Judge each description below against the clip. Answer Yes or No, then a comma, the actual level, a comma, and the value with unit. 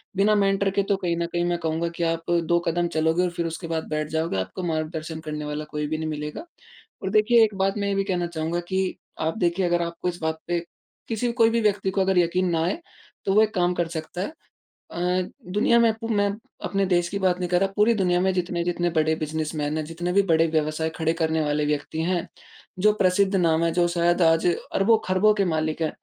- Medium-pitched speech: Yes, medium, 175 Hz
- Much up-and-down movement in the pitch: No, average, 3.2 semitones